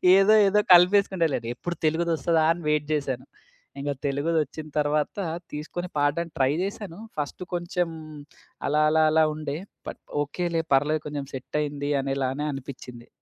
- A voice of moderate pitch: Yes, medium, 150 Hz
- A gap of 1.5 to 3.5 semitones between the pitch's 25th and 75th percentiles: Yes, average, 3.1 semitones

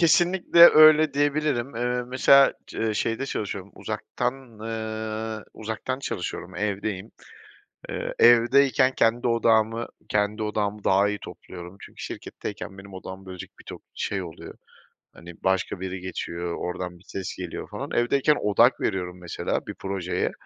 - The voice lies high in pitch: No, low, 110 Hz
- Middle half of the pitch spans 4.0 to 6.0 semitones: Yes, average, 4.4 semitones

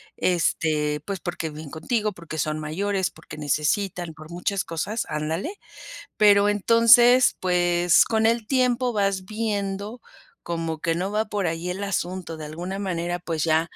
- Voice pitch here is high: No, medium, 180 Hz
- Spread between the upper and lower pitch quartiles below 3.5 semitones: No, average, 4.1 semitones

